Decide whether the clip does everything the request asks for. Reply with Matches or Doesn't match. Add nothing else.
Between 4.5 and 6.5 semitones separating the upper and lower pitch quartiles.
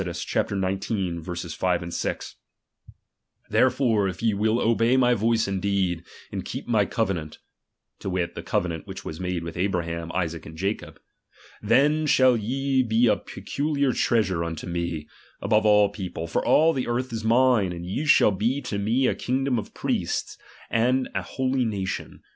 Matches